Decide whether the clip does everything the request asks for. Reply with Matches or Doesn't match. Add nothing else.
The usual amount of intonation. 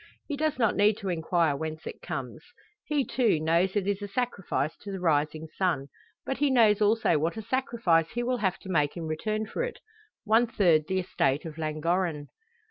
Doesn't match